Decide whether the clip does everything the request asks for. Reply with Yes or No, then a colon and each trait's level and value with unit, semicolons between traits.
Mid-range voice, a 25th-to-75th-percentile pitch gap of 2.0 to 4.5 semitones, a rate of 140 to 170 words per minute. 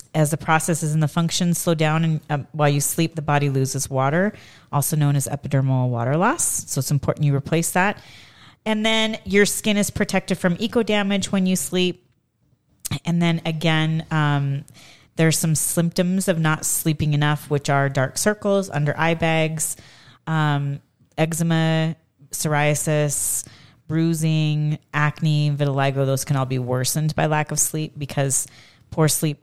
Yes: medium, 155 Hz; average, 2.9 semitones; average, 155 wpm